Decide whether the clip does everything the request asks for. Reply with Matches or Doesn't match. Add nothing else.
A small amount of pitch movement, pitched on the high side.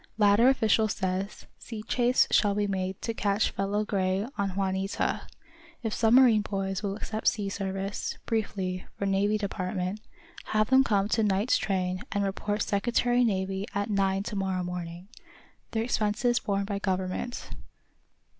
Matches